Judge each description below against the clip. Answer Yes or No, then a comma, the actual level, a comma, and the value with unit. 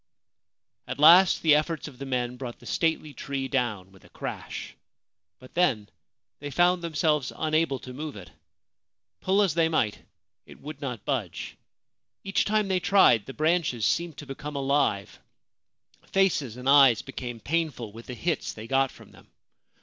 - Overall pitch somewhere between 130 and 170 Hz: Yes, medium, 140 Hz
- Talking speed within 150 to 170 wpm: Yes, average, 165 wpm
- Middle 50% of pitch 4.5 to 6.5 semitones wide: Yes, average, 4.8 semitones